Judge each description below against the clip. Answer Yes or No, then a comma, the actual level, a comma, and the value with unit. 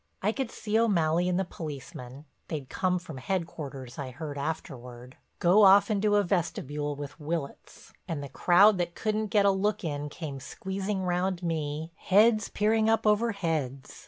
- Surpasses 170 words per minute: No, average, 165 wpm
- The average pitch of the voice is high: No, medium, 175 Hz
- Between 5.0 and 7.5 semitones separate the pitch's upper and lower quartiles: Yes, wide, 5.5 semitones